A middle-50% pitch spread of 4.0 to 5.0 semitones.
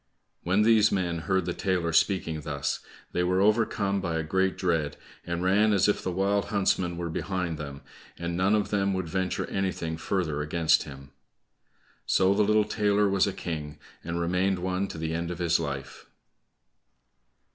No: average, 3.1 semitones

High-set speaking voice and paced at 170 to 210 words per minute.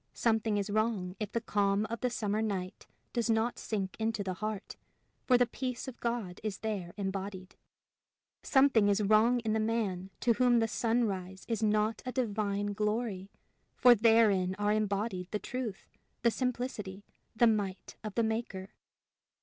No: high, 215 Hz; average, 160 wpm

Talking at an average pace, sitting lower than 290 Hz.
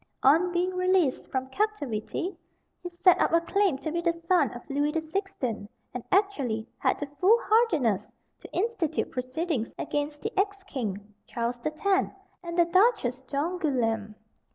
No: average, 155 wpm; very high, 320 Hz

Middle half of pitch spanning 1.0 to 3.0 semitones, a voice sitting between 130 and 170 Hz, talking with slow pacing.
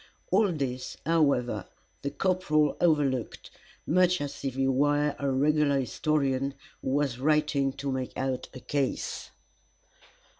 Yes: narrow, 2.4 semitones; medium, 140 Hz; slow, 125 wpm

